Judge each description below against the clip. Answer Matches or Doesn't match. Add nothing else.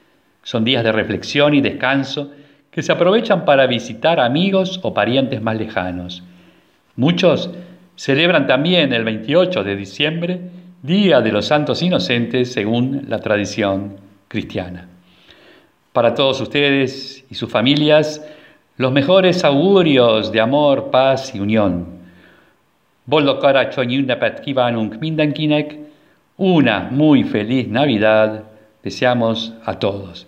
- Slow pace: Matches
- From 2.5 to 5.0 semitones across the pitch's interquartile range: Doesn't match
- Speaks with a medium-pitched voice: Doesn't match